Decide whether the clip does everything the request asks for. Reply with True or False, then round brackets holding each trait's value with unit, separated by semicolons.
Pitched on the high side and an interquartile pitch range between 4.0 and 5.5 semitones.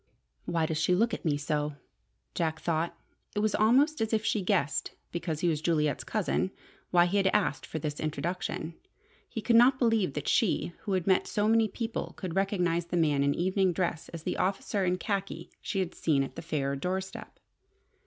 False (180 Hz; 4.4 semitones)